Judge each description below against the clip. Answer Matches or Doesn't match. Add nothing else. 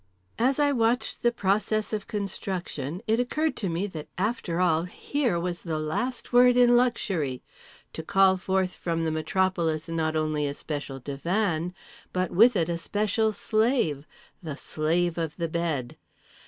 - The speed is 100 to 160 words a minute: Matches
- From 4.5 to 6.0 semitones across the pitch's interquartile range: Matches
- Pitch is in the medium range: Matches